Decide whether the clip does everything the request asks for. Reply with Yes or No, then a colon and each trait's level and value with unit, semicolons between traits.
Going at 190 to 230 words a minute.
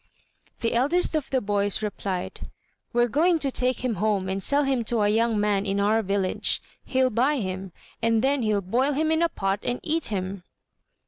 Yes: average, 195 wpm